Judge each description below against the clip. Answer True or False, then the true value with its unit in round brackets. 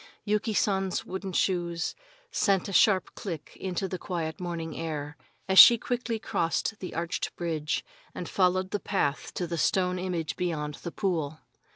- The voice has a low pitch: False (180 Hz)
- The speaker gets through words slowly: False (160 wpm)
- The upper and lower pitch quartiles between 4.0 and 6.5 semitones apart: False (2.7 semitones)